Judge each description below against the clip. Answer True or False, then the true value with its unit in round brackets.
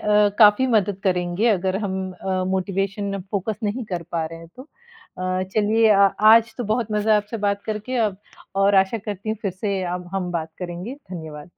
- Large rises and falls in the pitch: False (2.8 semitones)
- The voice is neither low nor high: False (200 Hz)